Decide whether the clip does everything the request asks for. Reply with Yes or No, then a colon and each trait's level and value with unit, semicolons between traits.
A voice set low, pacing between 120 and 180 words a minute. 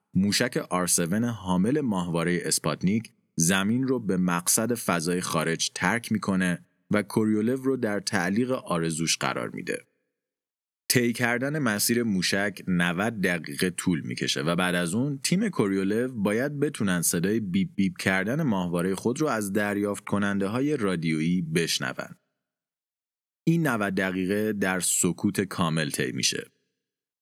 Yes: low, 100 Hz; average, 130 wpm